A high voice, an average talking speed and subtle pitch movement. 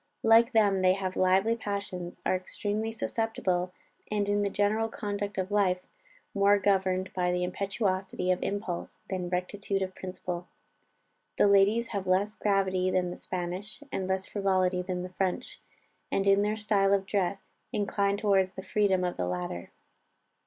Yes: high, 195 Hz; average, 160 wpm; narrow, 1.8 semitones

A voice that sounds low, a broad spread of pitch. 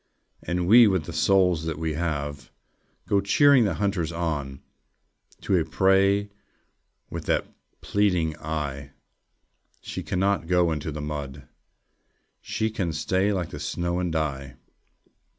No: very low, 85 Hz; average, 4.3 semitones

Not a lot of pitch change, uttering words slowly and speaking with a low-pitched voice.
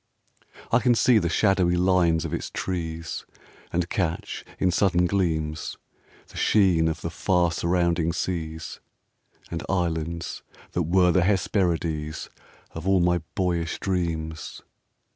Yes: narrow, 2.2 semitones; slow, 125 wpm; very low, 85 Hz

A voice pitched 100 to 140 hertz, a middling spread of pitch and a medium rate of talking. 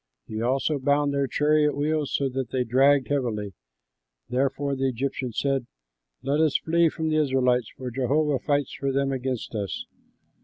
No: low, 135 Hz; narrow, 2.2 semitones; average, 160 wpm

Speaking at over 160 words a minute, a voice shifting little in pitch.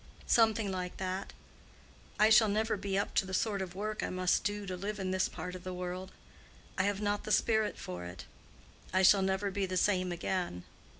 Yes: fast, 205 wpm; narrow, 2.1 semitones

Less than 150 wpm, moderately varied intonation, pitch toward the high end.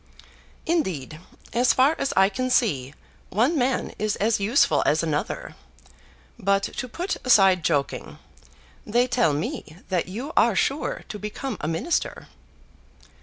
No: slow, 135 wpm; wide, 5.8 semitones; high, 215 Hz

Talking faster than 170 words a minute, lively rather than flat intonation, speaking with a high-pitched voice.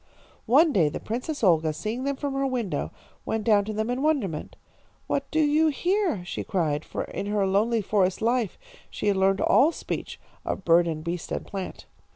Yes: average, 195 wpm; wide, 6.5 semitones; high, 215 Hz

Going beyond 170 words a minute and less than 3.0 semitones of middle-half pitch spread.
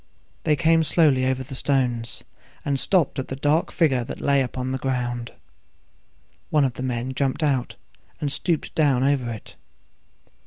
No: average, 160 wpm; narrow, 2.4 semitones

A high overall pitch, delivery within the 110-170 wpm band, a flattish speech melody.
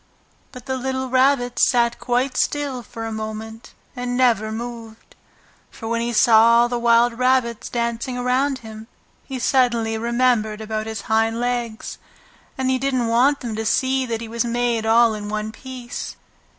Yes: high, 235 Hz; average, 165 wpm; narrow, 2.2 semitones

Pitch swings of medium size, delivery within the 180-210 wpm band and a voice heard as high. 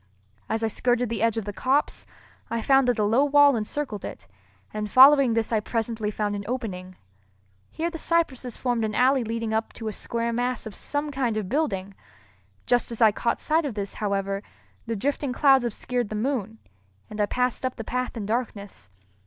Yes: average, 3.4 semitones; average, 195 wpm; high, 230 Hz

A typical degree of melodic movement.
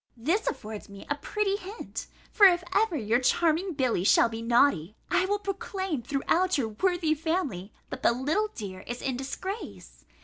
No: wide, 8.1 semitones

